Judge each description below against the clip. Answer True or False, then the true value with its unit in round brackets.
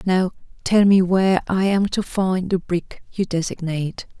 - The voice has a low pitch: False (185 Hz)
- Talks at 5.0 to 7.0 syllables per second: False (4.5 syllables/s)